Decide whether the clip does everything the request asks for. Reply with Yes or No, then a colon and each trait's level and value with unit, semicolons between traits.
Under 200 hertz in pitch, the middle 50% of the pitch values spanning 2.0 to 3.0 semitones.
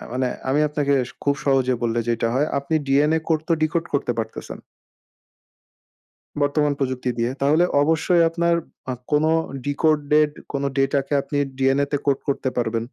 Yes: medium, 140 Hz; narrow, 2.4 semitones